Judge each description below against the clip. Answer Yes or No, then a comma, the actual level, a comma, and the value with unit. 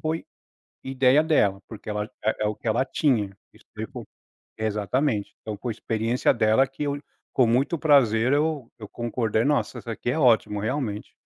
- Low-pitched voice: Yes, low, 120 Hz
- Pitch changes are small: No, average, 4.1 semitones